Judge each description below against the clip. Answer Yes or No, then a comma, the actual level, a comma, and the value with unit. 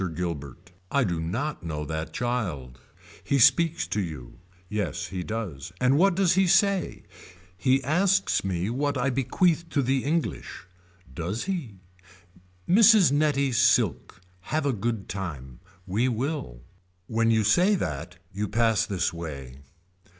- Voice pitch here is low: Yes, low, 115 Hz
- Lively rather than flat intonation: Yes, wide, 8.6 semitones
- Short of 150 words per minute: Yes, average, 140 wpm